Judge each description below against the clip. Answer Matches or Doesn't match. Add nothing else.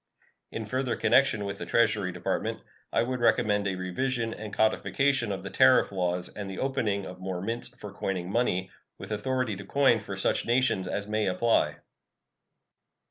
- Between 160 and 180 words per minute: Matches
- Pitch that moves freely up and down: Doesn't match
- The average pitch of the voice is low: Matches